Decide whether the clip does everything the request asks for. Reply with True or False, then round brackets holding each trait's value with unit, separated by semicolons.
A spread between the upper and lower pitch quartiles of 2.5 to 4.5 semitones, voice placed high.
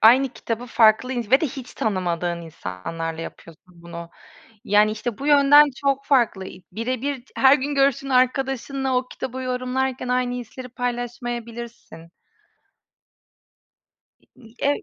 True (3.7 semitones; 245 Hz)